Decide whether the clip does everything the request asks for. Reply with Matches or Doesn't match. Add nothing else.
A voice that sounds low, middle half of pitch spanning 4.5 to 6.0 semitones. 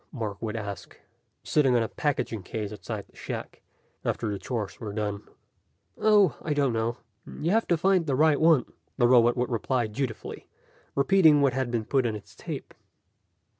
Matches